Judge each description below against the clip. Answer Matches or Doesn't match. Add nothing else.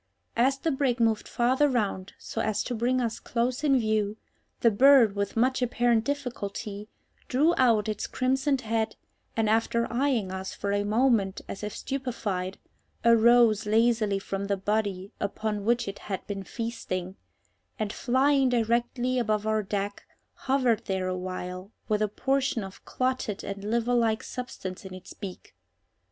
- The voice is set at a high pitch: Matches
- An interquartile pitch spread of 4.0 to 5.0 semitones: Doesn't match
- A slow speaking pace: Doesn't match